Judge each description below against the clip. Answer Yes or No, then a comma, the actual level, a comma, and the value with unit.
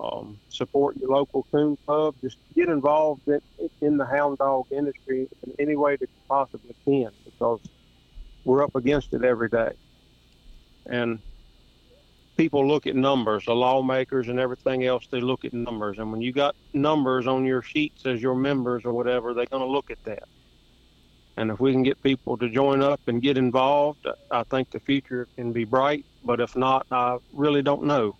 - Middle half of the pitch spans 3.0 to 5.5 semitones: No, narrow, 2.4 semitones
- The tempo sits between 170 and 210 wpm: Yes, average, 185 wpm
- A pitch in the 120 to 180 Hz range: Yes, low, 130 Hz